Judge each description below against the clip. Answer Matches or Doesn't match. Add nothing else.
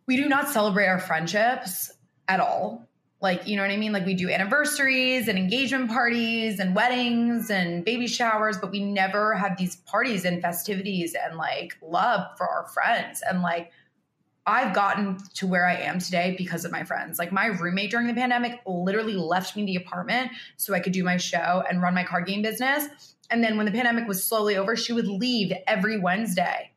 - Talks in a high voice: Matches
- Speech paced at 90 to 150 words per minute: Doesn't match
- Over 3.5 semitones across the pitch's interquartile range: Matches